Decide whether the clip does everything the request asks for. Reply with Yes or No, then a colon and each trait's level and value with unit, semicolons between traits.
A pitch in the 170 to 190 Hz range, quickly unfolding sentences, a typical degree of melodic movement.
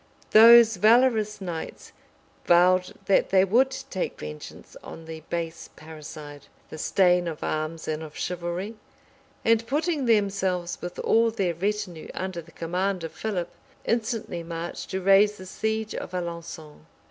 No: medium, 185 Hz; average, 140 wpm; average, 4.3 semitones